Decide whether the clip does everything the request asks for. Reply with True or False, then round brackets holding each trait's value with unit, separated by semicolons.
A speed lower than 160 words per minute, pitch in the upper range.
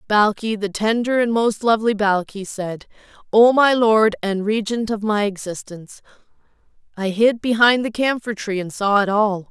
True (150 wpm; 215 Hz)